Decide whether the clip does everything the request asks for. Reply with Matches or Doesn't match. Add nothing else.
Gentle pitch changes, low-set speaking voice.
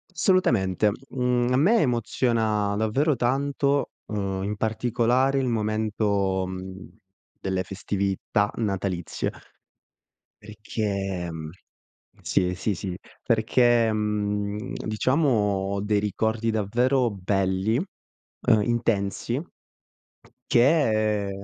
Doesn't match